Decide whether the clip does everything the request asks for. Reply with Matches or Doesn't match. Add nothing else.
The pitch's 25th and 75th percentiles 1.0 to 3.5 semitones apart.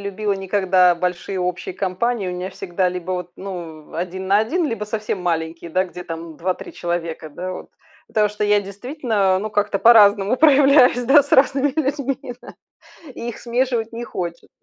Doesn't match